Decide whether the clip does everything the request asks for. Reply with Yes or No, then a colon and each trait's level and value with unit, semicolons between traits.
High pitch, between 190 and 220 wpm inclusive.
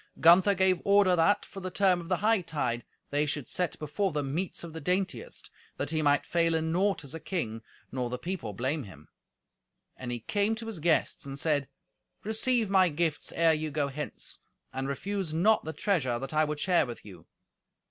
No: medium, 160 Hz; average, 200 wpm